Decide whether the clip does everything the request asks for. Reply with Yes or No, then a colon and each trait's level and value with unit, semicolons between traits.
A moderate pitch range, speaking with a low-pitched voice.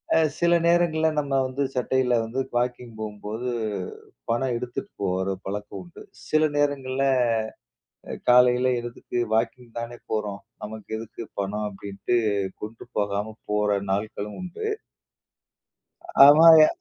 Yes: average, 4.0 semitones; low, 120 Hz